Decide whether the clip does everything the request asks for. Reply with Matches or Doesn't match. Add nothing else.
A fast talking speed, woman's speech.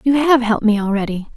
Matches